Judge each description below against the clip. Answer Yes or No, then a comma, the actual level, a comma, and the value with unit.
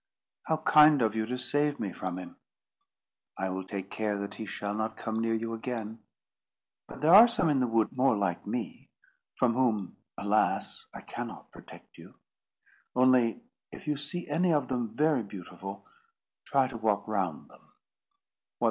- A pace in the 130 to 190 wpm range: Yes, average, 165 wpm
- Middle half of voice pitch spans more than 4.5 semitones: Yes, average, 5.0 semitones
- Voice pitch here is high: No, low, 115 Hz